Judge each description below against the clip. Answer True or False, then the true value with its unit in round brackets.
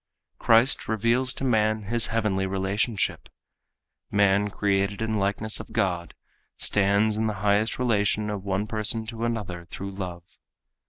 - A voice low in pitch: True (105 Hz)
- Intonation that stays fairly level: True (2.2 semitones)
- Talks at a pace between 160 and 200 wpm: False (145 wpm)